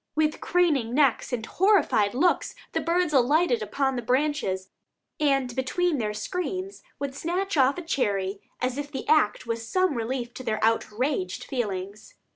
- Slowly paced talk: No, average, 155 wpm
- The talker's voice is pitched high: Yes, very high, 265 Hz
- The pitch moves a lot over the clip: Yes, wide, 5.8 semitones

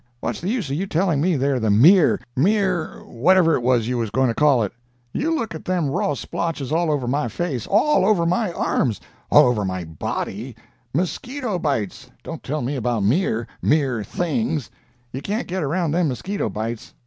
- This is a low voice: No, medium, 150 Hz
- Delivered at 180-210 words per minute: No, average, 170 wpm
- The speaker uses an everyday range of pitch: No, wide, 6.9 semitones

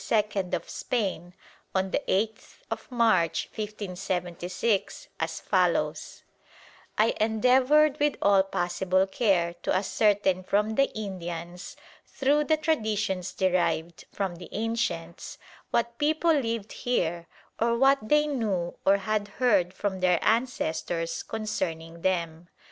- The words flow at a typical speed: No, slow, 115 wpm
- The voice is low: No, high, 200 Hz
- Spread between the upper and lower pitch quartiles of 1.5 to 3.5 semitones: No, average, 4.5 semitones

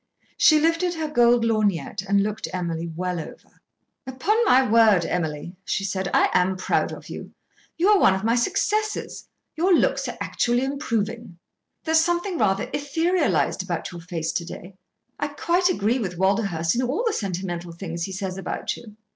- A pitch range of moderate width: No, wide, 8.7 semitones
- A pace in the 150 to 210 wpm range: Yes, average, 170 wpm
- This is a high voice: Yes, high, 215 Hz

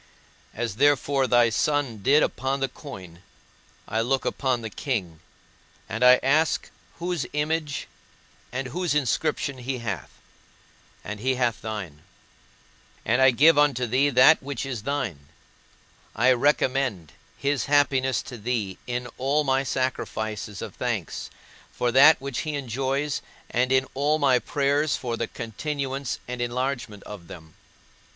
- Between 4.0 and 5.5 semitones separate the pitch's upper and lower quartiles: No, average, 3.3 semitones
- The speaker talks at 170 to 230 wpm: No, average, 140 wpm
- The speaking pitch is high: No, low, 130 Hz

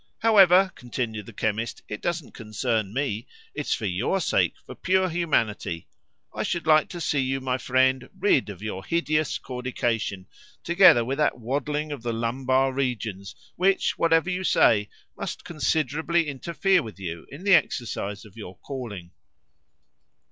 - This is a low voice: Yes, low, 130 Hz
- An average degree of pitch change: No, wide, 6.6 semitones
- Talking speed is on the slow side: No, average, 150 wpm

